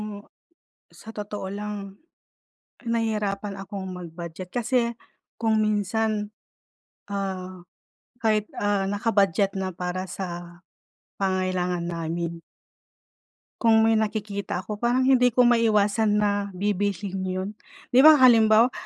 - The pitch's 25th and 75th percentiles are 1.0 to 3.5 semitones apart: Yes, average, 2.8 semitones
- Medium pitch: No, high, 205 Hz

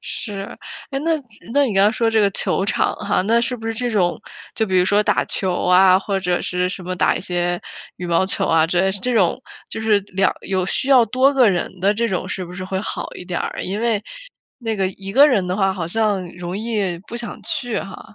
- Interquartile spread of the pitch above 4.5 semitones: No, average, 3.6 semitones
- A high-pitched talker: Yes, high, 195 Hz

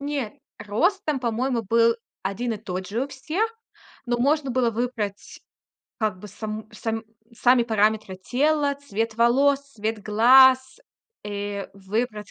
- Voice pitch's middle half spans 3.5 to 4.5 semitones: Yes, average, 3.8 semitones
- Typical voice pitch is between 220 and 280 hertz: Yes, high, 230 Hz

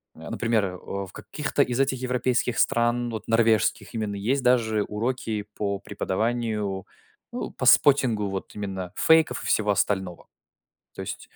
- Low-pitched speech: Yes, low, 110 Hz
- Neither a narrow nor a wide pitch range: Yes, average, 3.5 semitones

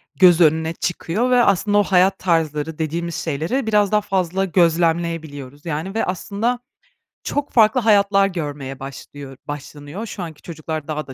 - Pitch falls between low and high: Yes, medium, 170 Hz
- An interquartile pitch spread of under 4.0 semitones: No, average, 4.6 semitones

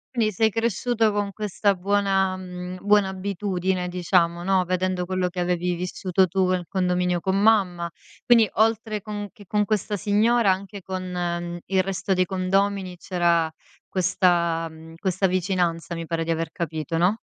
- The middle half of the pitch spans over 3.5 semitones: No, narrow, 2.4 semitones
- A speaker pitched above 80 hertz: Yes, medium, 185 Hz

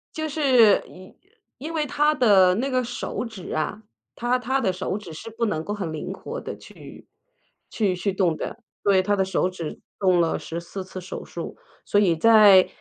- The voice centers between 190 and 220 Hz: Yes, high, 200 Hz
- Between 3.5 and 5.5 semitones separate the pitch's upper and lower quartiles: Yes, average, 4.9 semitones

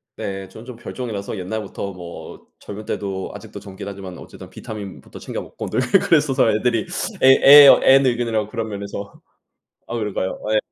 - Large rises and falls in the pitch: No, average, 3.4 semitones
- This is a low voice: Yes, low, 105 Hz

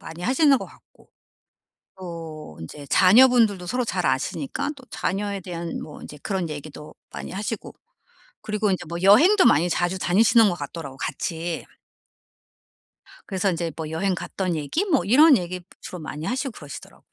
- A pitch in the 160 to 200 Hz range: Yes, medium, 185 Hz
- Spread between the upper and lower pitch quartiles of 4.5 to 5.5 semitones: Yes, average, 5.2 semitones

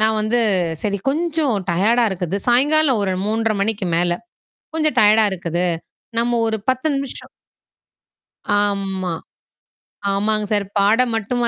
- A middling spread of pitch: Yes, average, 3.7 semitones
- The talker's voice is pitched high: Yes, high, 220 Hz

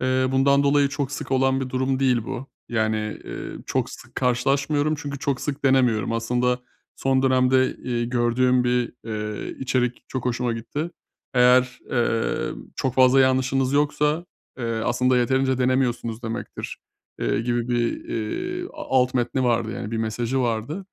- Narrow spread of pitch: Yes, narrow, 2.0 semitones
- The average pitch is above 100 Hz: Yes, low, 125 Hz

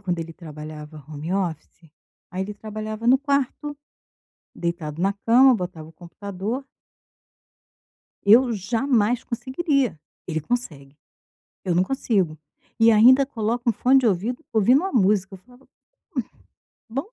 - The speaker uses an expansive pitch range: Yes, wide, 6.3 semitones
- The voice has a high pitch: Yes, high, 210 Hz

